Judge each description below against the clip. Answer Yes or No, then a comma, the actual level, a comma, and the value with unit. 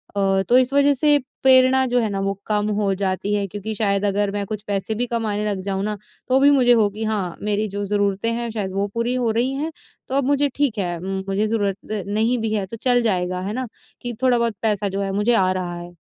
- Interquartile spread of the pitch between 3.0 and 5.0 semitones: Yes, average, 3.5 semitones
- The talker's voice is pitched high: Yes, high, 210 Hz